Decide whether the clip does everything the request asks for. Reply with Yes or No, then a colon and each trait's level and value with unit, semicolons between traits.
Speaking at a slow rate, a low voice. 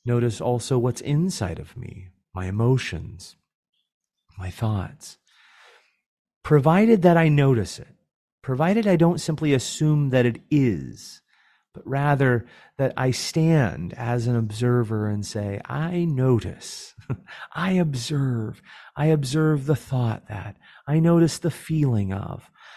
Yes: slow, 125 wpm; low, 130 Hz